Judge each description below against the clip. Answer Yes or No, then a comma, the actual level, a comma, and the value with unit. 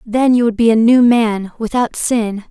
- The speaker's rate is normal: No, fast, 215 wpm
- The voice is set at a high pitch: Yes, high, 230 Hz